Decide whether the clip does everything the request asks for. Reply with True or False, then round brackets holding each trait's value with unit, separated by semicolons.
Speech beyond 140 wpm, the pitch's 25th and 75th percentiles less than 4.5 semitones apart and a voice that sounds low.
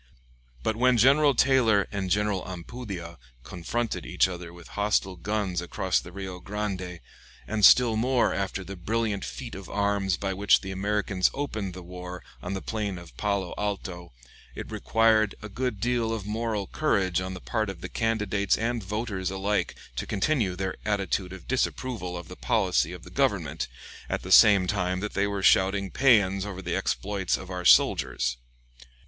True (170 wpm; 2.9 semitones; 100 Hz)